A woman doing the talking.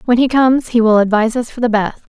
Yes: female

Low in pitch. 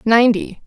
No: high, 225 Hz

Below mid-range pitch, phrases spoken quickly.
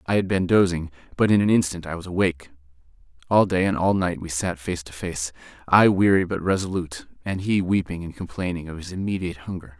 Yes: very low, 90 Hz; fast, 210 wpm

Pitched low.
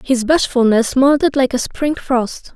No: very high, 260 Hz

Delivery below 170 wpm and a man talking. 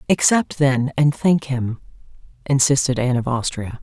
No: average, 140 wpm; female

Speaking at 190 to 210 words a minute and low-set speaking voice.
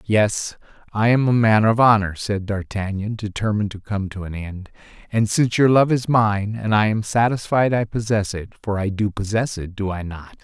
Yes: average, 200 wpm; low, 105 Hz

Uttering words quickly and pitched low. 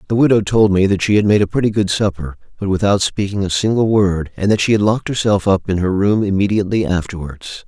Yes: fast, 235 wpm; low, 100 Hz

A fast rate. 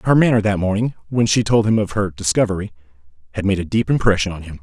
Yes: fast, 235 wpm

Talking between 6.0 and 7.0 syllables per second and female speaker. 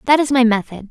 Yes: 6.5 syllables/s; female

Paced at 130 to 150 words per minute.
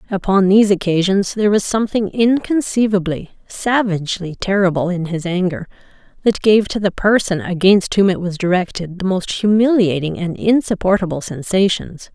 Yes: average, 140 wpm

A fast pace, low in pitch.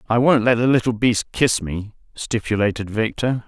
No: average, 175 wpm; low, 115 Hz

